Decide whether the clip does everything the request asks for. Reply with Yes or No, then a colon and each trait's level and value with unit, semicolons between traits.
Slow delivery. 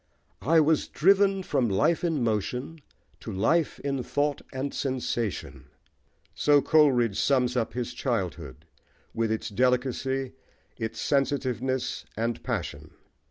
Yes: slow, 115 wpm